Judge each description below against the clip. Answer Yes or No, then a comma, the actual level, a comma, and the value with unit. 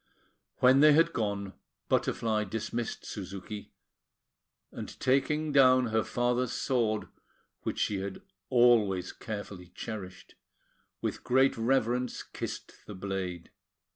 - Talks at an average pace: No, slow, 110 wpm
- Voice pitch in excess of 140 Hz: No, low, 110 Hz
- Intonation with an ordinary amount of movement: Yes, average, 4.2 semitones